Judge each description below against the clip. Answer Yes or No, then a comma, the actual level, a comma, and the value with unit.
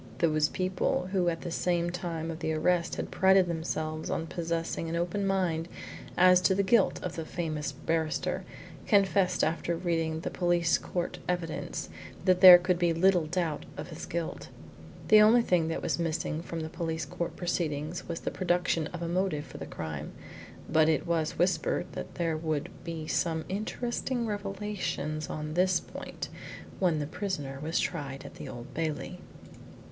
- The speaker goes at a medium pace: Yes, average, 170 wpm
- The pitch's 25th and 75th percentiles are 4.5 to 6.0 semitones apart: No, narrow, 2.4 semitones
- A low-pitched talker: No, medium, 170 Hz